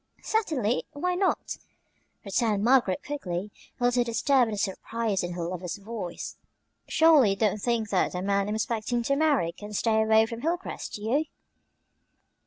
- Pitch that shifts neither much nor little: Yes, average, 4.4 semitones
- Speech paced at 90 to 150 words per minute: No, average, 165 wpm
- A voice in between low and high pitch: No, high, 220 Hz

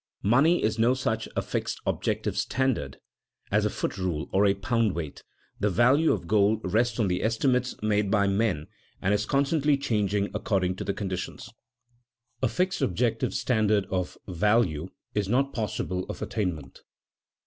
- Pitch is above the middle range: No, low, 105 Hz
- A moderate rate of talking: Yes, average, 155 wpm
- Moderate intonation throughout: Yes, average, 4.0 semitones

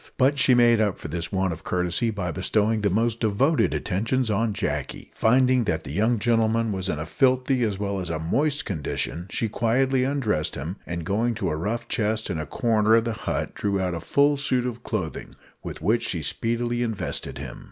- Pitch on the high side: No, low, 110 Hz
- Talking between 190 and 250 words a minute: Yes, fast, 205 wpm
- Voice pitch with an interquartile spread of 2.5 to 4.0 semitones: No, average, 4.7 semitones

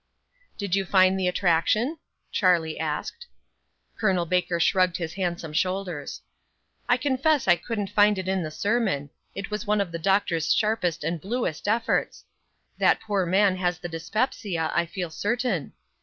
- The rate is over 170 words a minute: No, average, 155 wpm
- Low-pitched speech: No, medium, 185 Hz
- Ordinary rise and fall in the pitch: Yes, average, 3.6 semitones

